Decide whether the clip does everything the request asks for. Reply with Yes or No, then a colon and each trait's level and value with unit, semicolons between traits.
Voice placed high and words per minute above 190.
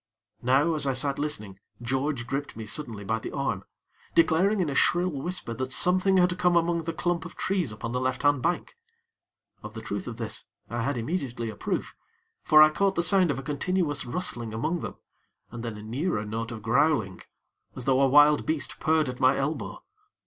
No: medium, 140 Hz; average, 200 wpm